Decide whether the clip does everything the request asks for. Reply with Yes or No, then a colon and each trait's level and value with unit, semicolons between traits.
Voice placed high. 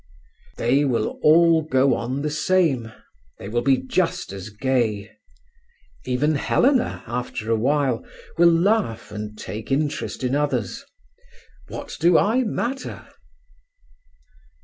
No: low, 135 Hz